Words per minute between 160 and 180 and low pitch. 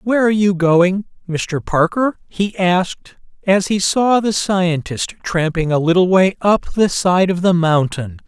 No: average, 165 wpm; medium, 180 Hz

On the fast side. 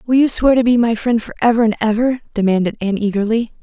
Yes: fast, 215 wpm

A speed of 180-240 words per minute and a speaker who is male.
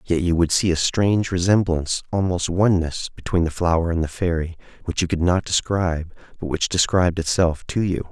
Yes: average, 190 wpm; male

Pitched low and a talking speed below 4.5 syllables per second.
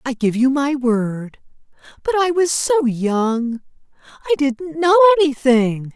No: very high, 275 Hz; 3.8 syllables/s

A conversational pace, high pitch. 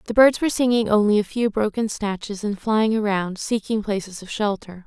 Yes: average, 195 wpm; high, 210 Hz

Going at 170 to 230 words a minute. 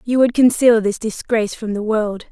Yes: fast, 205 wpm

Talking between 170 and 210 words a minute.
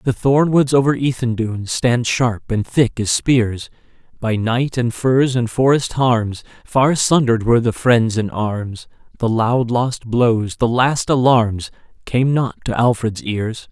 No: average, 160 wpm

